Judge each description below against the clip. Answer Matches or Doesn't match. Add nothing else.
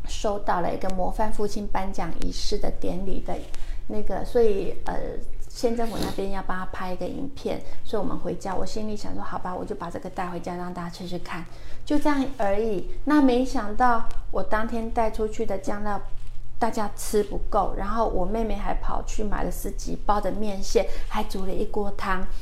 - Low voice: Doesn't match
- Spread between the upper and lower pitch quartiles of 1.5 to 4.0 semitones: Matches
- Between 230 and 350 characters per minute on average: Matches